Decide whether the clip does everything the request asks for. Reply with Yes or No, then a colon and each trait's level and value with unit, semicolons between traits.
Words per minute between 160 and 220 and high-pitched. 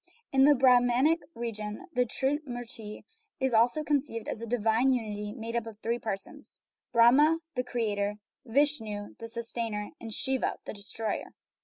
No: average, 145 wpm; high, 235 Hz